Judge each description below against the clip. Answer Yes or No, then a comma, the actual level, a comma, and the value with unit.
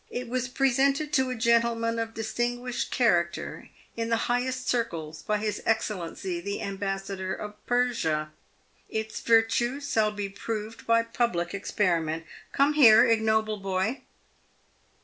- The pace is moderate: No, slow, 130 wpm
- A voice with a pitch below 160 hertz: No, high, 225 Hz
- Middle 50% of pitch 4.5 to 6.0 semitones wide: No, average, 3.4 semitones